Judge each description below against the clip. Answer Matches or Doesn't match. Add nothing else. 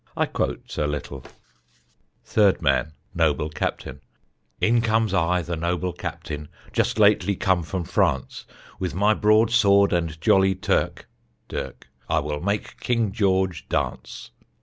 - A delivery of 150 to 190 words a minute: Doesn't match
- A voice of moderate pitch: Doesn't match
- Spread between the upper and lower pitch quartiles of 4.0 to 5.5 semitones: Matches